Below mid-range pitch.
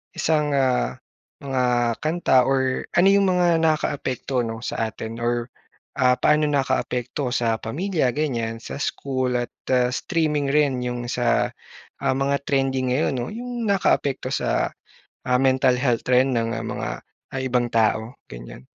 Yes: low, 130 Hz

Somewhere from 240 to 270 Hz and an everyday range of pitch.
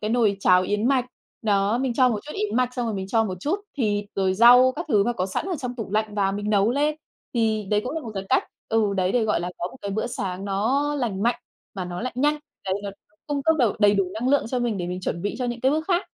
No: high, 225 Hz; average, 4.3 semitones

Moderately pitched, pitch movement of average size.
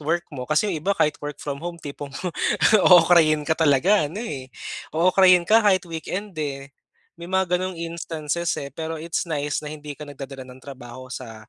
Yes: medium, 155 Hz; average, 3.5 semitones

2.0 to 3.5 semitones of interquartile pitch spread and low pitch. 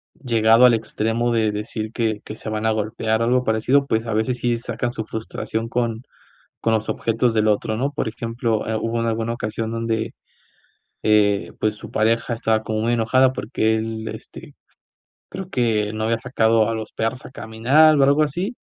No: narrow, 1.5 semitones; low, 115 Hz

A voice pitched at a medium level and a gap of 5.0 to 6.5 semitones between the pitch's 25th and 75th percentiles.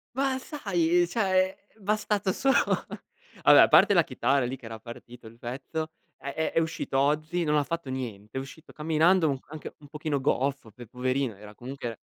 Yes: medium, 150 Hz; average, 5.3 semitones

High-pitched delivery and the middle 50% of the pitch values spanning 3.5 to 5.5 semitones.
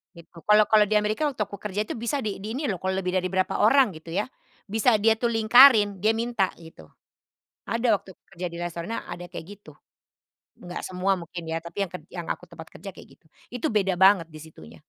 Yes: high, 195 Hz; average, 3.8 semitones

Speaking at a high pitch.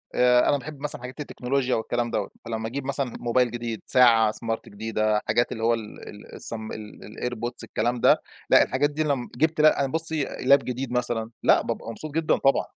No: low, 125 Hz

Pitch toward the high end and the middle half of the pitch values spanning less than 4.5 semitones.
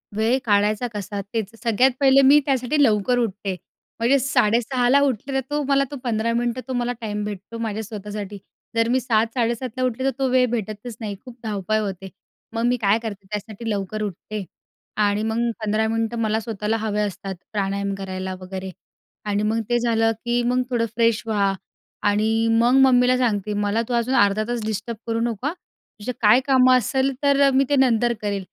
Yes: high, 225 Hz; average, 3.0 semitones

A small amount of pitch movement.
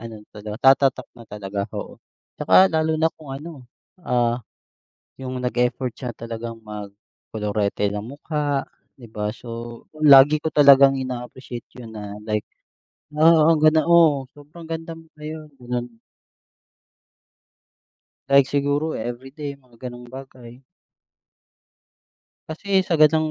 No: average, 4.6 semitones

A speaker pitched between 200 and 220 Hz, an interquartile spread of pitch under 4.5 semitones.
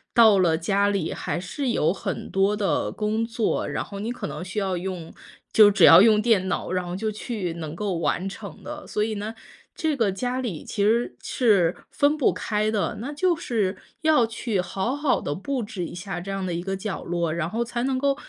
Yes: high, 205 Hz; average, 4.1 semitones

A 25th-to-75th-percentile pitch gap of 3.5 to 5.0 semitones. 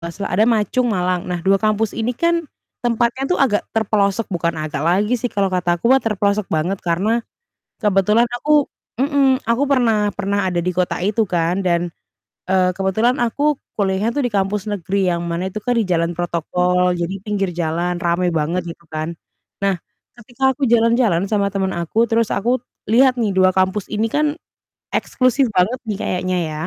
Yes: average, 4.5 semitones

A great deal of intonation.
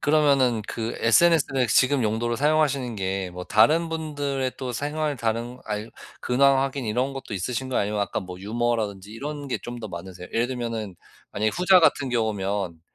No: average, 4.6 semitones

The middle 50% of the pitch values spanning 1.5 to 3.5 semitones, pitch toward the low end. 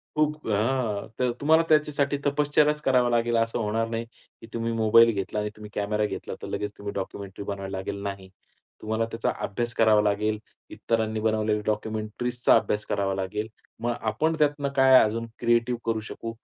Yes: average, 2.8 semitones; low, 115 Hz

